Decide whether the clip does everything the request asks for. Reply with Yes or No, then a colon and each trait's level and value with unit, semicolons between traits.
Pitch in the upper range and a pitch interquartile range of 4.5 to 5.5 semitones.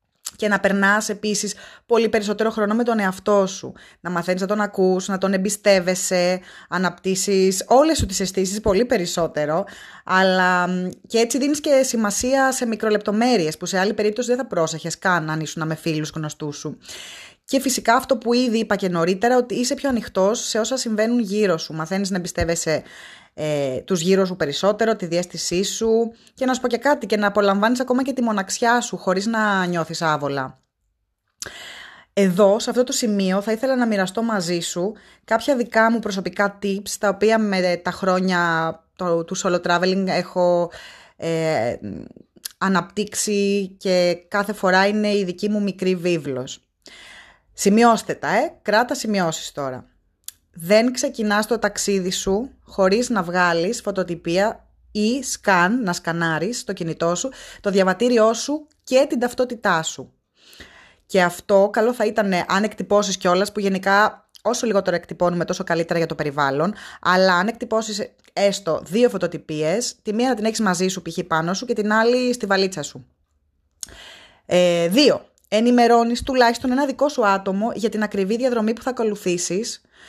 No: high, 200 Hz; average, 4.1 semitones